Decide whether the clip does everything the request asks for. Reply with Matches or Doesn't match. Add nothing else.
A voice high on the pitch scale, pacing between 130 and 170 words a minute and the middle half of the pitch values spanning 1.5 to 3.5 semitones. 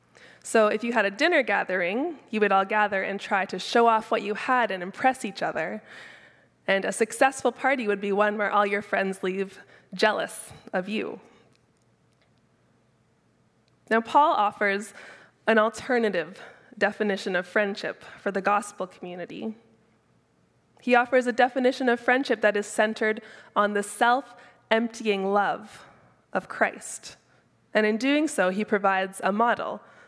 Matches